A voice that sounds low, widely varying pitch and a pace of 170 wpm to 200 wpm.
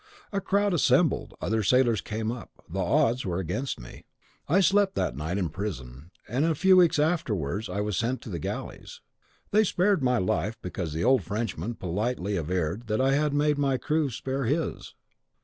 Yes: low, 115 Hz; wide, 8.2 semitones; average, 185 wpm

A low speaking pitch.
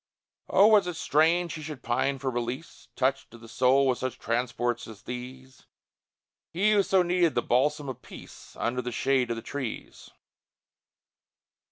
Yes: low, 130 Hz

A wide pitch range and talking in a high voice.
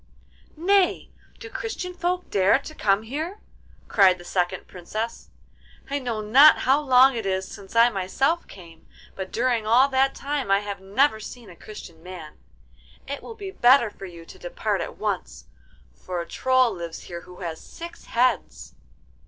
Yes: wide, 6.8 semitones; high, 230 Hz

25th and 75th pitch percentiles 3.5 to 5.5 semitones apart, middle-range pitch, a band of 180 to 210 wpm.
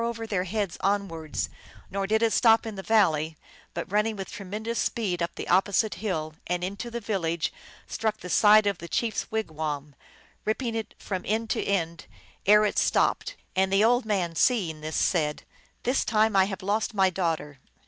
No: average, 4.3 semitones; high, 200 Hz; average, 200 wpm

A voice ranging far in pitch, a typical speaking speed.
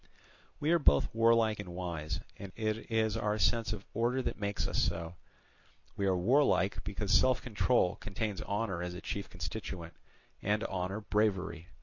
No: average, 3.5 semitones; average, 160 wpm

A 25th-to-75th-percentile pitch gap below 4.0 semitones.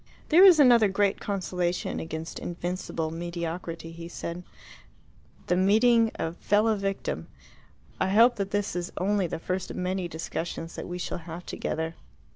Yes: average, 3.3 semitones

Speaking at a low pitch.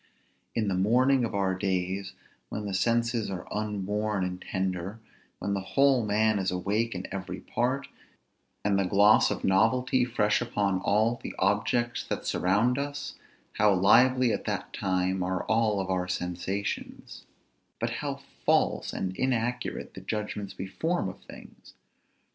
Yes: low, 105 Hz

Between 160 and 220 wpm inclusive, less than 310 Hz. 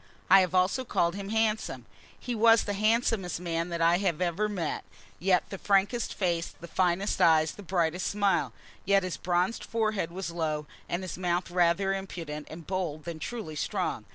Yes: average, 180 wpm; medium, 185 Hz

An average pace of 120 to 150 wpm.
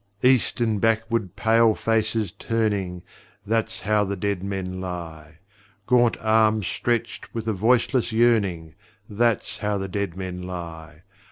Yes: slow, 135 wpm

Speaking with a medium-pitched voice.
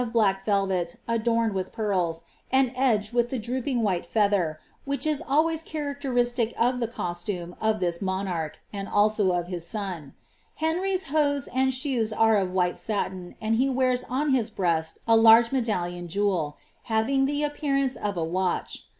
No: high, 220 Hz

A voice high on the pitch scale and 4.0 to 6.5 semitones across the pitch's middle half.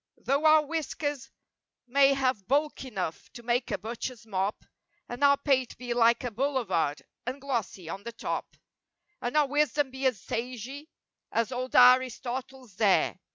No: very high, 255 Hz; average, 3.2 semitones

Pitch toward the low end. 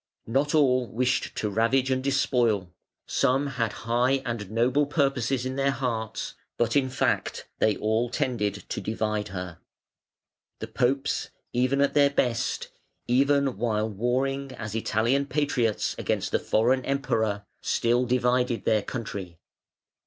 Yes: low, 125 Hz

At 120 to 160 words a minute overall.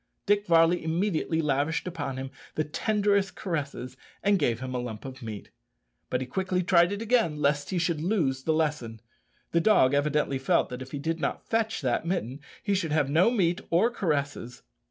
No: average, 190 wpm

